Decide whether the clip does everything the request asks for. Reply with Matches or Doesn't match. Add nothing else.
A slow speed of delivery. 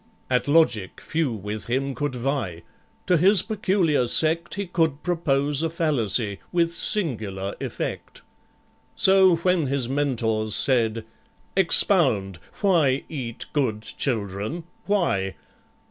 Matches